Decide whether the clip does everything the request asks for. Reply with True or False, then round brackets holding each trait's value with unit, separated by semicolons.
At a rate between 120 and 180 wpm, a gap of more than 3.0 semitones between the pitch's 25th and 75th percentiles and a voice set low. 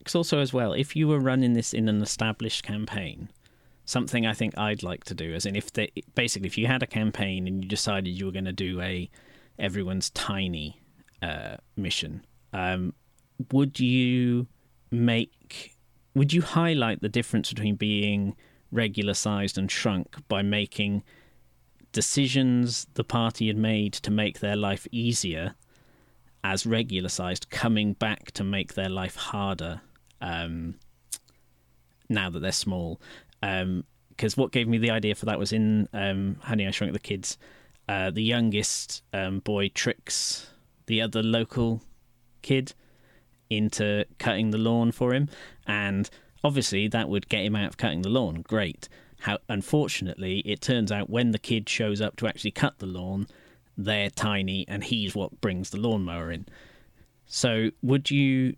True (160 wpm; 3.6 semitones; 105 Hz)